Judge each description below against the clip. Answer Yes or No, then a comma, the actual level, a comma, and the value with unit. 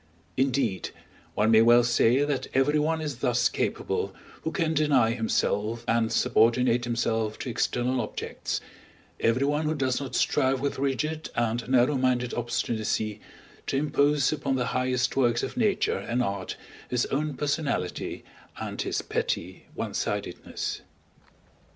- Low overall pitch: Yes, low, 125 Hz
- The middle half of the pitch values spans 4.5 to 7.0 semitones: No, average, 3.5 semitones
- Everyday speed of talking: No, slow, 130 wpm